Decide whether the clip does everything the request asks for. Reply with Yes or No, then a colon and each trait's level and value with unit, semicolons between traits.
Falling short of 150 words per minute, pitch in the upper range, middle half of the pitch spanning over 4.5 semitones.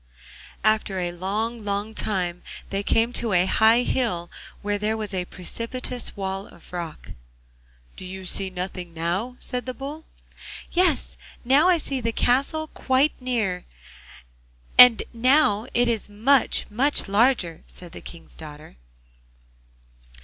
Yes: slow, 135 wpm; high, 215 Hz; average, 5.2 semitones